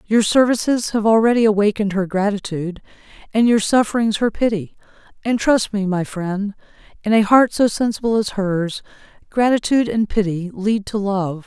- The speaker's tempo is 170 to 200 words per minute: No, average, 155 wpm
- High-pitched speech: Yes, high, 210 Hz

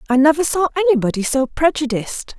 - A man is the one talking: No, female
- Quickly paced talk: No, average, 150 wpm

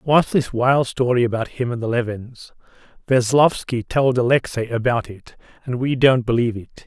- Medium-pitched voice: No, low, 125 Hz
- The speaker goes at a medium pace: Yes, average, 165 wpm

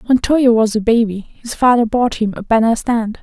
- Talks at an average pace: No, fast, 225 wpm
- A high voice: Yes, high, 230 Hz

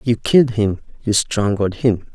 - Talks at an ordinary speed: Yes, average, 170 wpm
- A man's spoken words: Yes, male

